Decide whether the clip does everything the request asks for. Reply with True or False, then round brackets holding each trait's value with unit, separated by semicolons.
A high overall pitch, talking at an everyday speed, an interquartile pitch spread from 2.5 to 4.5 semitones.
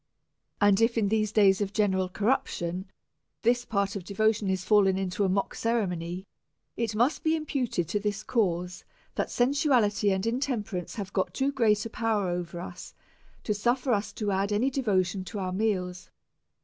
True (205 Hz; 170 wpm; 3.3 semitones)